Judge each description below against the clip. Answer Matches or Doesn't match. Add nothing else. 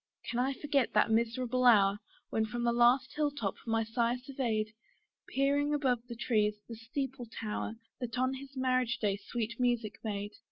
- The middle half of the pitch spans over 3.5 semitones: Doesn't match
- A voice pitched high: Matches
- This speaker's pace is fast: Doesn't match